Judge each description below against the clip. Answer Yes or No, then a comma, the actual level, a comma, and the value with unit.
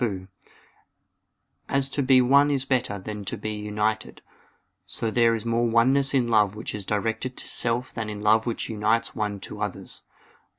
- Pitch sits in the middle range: No, low, 115 Hz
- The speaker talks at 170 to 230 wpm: Yes, average, 175 wpm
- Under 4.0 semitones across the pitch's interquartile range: Yes, average, 2.9 semitones